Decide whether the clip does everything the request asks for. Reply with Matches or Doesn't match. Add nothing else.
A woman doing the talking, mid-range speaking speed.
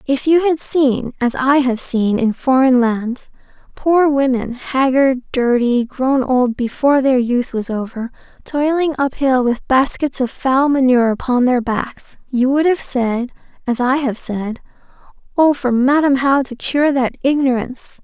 Matches